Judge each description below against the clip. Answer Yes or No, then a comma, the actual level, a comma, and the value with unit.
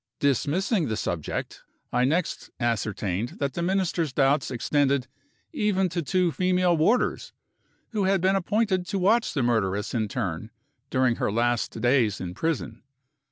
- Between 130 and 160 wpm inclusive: Yes, average, 150 wpm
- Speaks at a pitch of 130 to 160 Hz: Yes, medium, 140 Hz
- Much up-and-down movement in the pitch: Yes, wide, 7.8 semitones